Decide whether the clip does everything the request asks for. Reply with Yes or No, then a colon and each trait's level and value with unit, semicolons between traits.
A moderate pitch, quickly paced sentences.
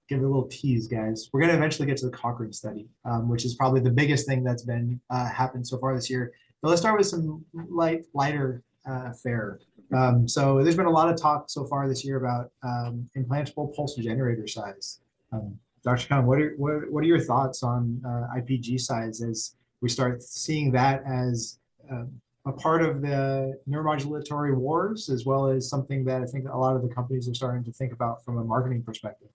No: low, 130 Hz; fast, 215 wpm